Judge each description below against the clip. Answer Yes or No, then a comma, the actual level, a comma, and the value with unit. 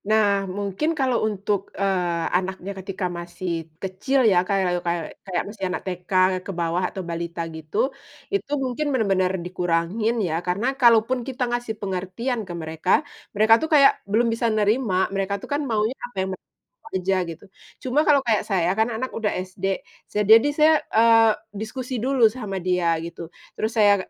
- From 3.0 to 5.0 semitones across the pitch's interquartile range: Yes, average, 4.2 semitones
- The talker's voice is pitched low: No, high, 200 Hz